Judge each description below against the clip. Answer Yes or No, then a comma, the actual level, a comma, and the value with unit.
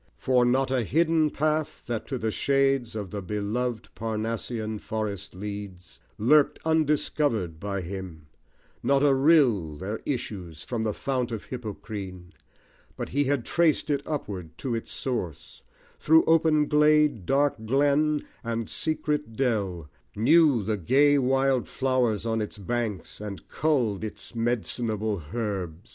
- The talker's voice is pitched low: Yes, low, 115 Hz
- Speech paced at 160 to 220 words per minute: No, slow, 135 wpm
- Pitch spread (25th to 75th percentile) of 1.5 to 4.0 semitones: No, wide, 5.5 semitones